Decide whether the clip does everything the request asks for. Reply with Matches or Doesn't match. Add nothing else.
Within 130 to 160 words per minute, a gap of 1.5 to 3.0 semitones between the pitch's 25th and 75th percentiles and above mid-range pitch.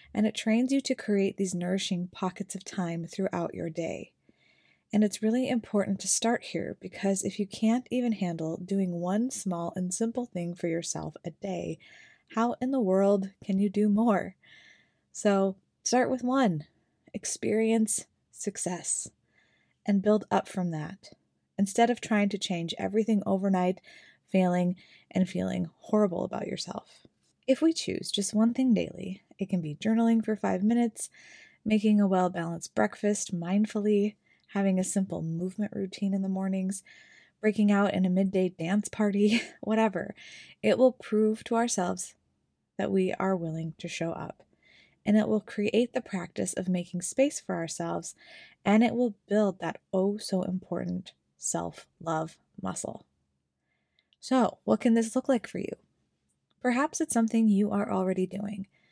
Doesn't match